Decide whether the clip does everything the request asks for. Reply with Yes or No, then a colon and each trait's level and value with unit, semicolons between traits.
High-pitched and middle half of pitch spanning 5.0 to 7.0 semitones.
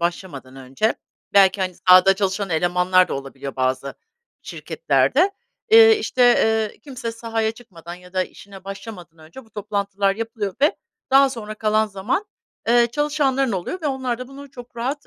Yes: high, 210 Hz; average, 5.3 semitones